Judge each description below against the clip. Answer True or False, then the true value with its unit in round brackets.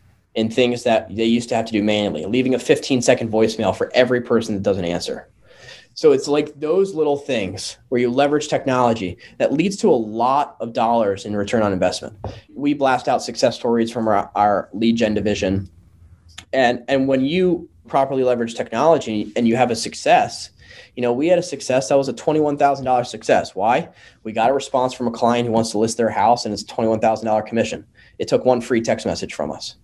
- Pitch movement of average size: True (3.4 semitones)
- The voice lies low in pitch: True (115 Hz)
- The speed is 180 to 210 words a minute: True (205 wpm)